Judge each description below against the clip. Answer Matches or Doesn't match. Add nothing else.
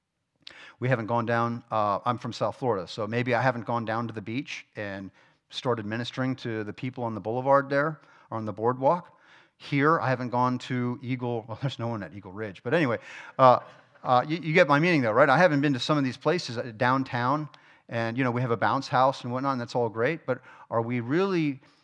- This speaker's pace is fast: Matches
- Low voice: Matches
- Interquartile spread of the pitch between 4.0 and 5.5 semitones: Doesn't match